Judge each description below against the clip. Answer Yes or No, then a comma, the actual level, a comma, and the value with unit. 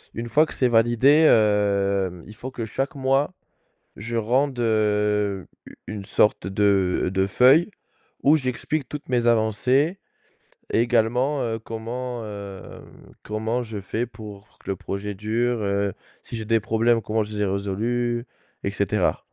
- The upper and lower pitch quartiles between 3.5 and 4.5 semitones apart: No, average, 3.1 semitones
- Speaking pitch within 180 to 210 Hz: No, low, 110 Hz